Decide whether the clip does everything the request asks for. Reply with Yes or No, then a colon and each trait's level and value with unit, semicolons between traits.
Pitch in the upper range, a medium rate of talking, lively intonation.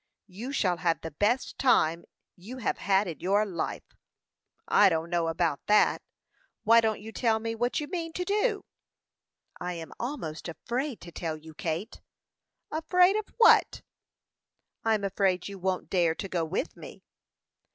Yes: high, 200 Hz; average, 160 wpm; wide, 6.2 semitones